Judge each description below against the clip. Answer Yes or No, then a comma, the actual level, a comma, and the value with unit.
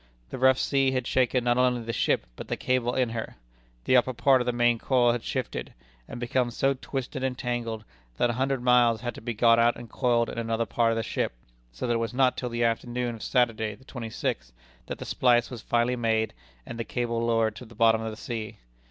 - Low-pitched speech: Yes, low, 120 Hz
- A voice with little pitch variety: Yes, narrow, 1.6 semitones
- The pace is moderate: No, fast, 240 wpm